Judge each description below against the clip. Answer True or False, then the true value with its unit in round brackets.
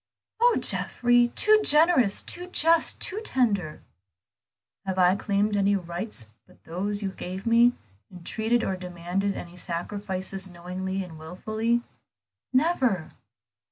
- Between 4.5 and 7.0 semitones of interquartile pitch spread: True (4.8 semitones)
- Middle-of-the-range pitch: False (200 Hz)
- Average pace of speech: False (120 wpm)